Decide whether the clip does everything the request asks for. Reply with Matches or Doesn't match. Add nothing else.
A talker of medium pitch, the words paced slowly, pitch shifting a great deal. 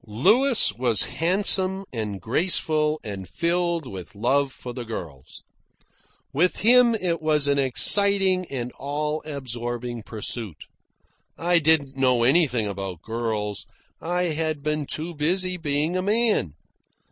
Matches